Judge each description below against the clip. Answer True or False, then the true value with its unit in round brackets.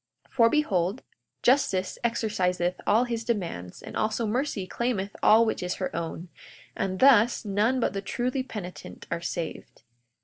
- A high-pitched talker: True (210 Hz)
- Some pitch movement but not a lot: True (4.6 semitones)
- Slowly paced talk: False (150 wpm)